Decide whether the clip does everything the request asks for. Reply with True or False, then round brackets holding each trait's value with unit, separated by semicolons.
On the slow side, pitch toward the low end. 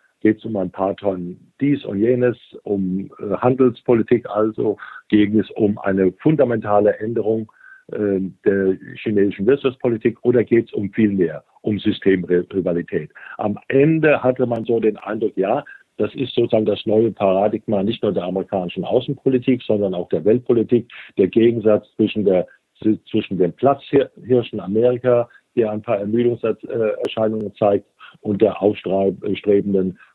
False (140 wpm; 105 Hz)